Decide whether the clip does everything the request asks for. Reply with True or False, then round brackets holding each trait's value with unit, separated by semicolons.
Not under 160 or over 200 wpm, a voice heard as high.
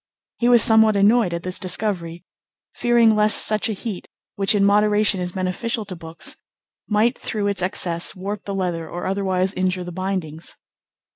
True (165 wpm; 195 Hz)